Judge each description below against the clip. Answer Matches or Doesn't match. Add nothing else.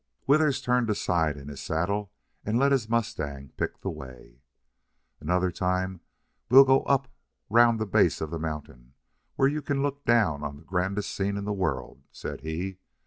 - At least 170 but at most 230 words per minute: Matches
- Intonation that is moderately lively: Doesn't match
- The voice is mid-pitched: Doesn't match